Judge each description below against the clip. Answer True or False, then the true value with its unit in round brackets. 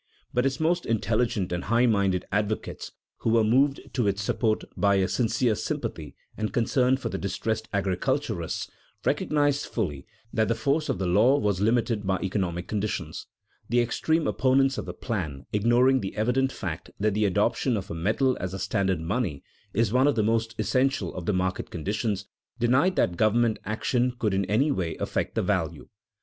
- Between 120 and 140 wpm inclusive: False (180 wpm)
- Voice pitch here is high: False (110 Hz)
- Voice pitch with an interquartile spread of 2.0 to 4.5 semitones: True (4.2 semitones)